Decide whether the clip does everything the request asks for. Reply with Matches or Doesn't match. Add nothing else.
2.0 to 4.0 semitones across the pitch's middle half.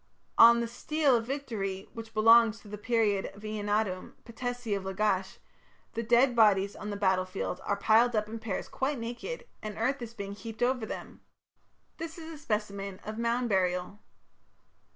Matches